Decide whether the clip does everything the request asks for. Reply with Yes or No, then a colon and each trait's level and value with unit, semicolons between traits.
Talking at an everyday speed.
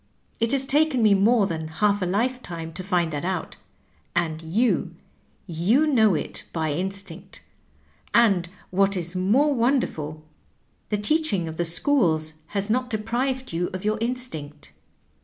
Yes: average, 150 wpm